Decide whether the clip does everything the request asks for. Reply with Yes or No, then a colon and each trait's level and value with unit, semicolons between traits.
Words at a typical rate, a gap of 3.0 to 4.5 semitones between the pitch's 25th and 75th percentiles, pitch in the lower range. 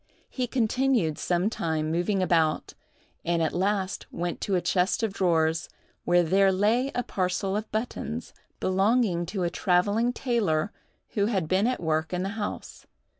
No: average, 160 wpm; average, 3.9 semitones; high, 190 Hz